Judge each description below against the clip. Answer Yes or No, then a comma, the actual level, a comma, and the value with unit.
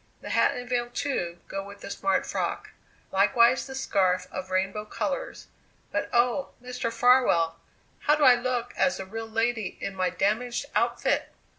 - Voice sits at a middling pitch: No, high, 230 Hz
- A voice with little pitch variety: No, average, 4.4 semitones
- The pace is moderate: Yes, average, 165 wpm